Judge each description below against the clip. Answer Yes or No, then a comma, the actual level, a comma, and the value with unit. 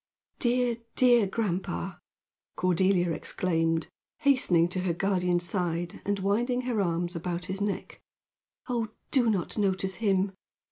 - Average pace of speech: No, slow, 125 wpm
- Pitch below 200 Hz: Yes, high, 190 Hz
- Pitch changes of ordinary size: Yes, average, 4.2 semitones